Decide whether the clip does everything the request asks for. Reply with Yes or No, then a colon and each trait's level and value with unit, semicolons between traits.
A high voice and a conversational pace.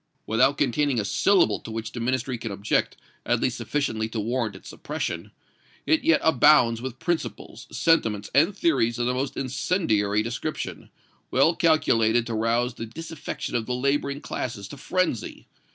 No: low, 125 Hz; average, 160 wpm